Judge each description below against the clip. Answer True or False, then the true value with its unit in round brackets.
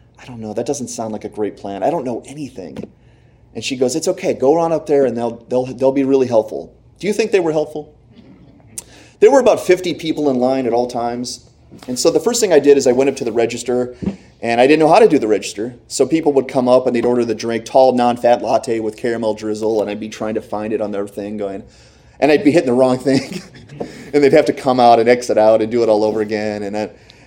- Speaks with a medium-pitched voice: False (120 Hz)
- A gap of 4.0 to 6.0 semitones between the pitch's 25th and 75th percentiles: False (3.6 semitones)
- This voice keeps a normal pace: False (265 wpm)